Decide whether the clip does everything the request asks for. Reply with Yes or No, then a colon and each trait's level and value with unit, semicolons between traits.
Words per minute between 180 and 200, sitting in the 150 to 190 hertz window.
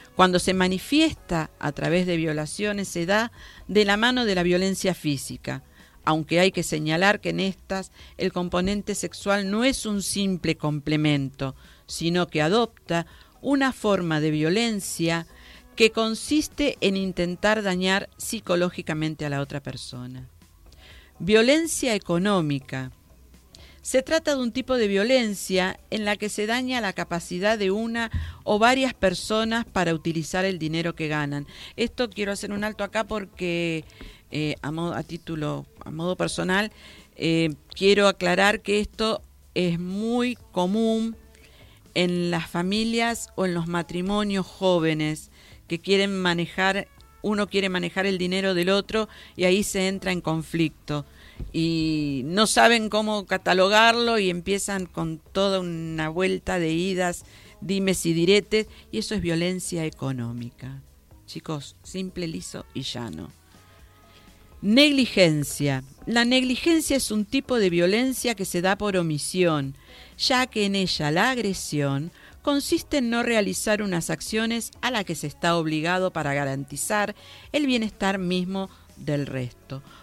No: average, 140 wpm; medium, 185 Hz